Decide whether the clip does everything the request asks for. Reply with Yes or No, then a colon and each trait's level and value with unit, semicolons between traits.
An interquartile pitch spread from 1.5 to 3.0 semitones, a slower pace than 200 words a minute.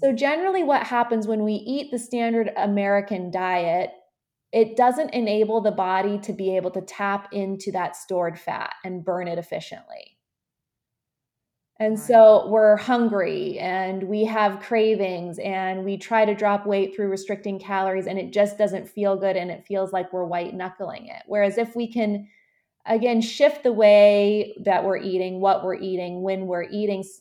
Yes: average, 2.7 semitones; average, 170 wpm